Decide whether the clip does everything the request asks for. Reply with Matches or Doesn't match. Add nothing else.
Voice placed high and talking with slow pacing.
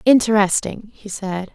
Matches